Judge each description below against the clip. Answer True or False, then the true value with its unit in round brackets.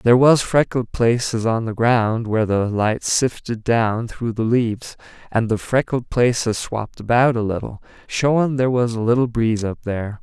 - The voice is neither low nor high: False (115 Hz)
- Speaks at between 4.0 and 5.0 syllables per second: True (4.9 syllables/s)